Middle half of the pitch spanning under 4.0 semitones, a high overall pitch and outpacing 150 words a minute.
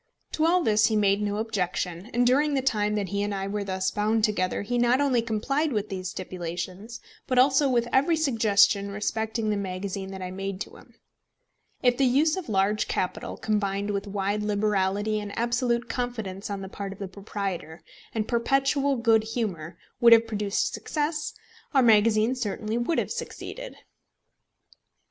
Yes: average, 3.6 semitones; high, 215 Hz; average, 170 wpm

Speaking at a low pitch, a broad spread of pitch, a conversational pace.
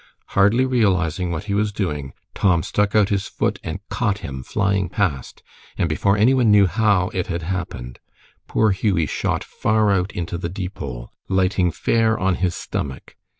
No: very low, 95 Hz; average, 3.3 semitones; average, 170 wpm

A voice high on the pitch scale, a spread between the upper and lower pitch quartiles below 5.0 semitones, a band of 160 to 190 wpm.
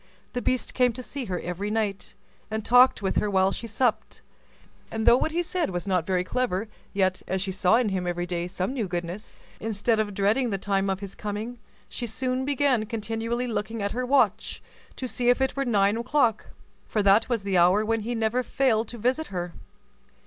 No: high, 220 Hz; average, 4.0 semitones; fast, 205 wpm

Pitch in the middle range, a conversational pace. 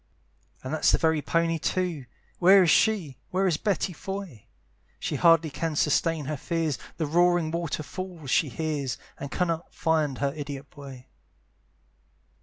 Yes: medium, 160 Hz; average, 150 wpm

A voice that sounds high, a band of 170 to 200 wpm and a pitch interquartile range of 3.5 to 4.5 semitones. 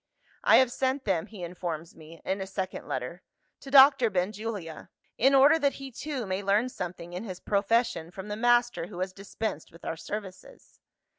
No: high, 200 Hz; average, 180 wpm; average, 5.3 semitones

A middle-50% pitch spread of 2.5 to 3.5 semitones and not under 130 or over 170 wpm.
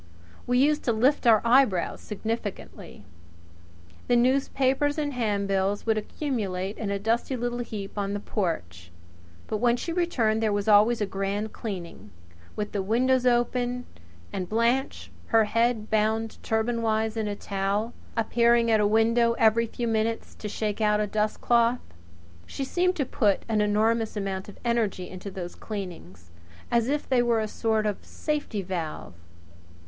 Yes: average, 2.8 semitones; average, 155 wpm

